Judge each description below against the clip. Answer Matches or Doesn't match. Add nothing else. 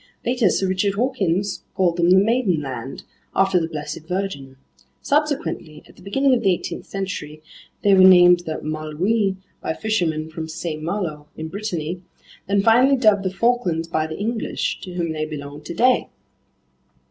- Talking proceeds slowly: Doesn't match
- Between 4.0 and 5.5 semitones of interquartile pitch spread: Matches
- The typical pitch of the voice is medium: Matches